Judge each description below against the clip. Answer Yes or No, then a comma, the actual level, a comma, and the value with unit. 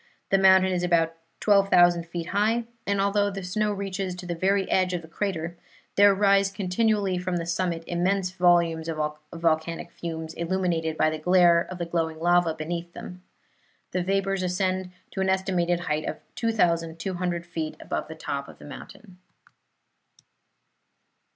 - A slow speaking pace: No, average, 155 wpm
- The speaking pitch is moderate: Yes, medium, 180 Hz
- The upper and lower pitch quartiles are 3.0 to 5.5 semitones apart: No, narrow, 2.4 semitones